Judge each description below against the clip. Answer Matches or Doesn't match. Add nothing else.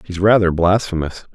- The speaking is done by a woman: Doesn't match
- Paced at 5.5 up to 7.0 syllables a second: Doesn't match